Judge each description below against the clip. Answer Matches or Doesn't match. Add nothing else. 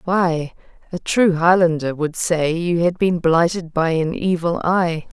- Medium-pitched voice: Matches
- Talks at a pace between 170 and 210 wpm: Doesn't match